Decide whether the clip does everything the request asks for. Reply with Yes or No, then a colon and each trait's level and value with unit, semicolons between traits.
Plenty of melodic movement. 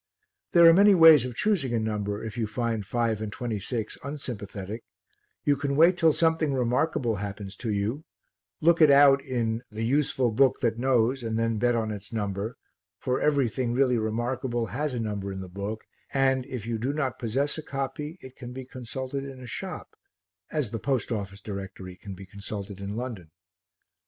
No: average, 4.2 semitones